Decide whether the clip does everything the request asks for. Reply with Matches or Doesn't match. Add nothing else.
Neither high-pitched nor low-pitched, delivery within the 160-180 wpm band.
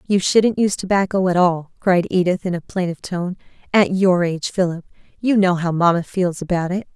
Doesn't match